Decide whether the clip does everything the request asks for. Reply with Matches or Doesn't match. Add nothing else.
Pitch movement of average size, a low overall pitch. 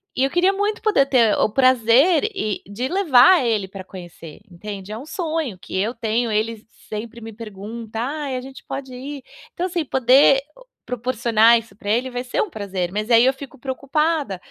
Doesn't match